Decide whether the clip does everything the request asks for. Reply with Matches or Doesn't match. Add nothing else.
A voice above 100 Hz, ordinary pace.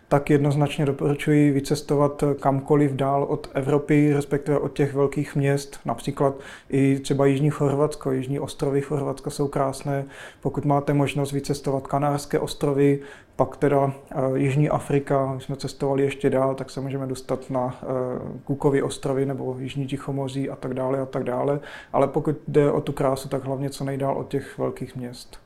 Matches